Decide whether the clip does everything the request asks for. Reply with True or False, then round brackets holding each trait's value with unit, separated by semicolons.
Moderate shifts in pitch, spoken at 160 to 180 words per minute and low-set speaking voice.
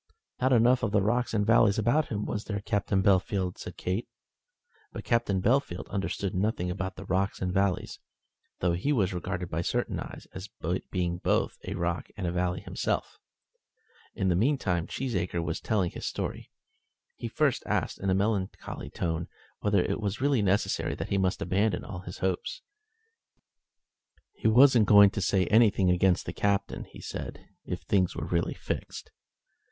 True (3.0 semitones; 170 wpm; 100 Hz)